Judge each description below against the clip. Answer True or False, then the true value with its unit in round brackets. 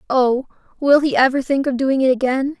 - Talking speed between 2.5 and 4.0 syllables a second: False (5.3 syllables/s)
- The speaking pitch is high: True (265 Hz)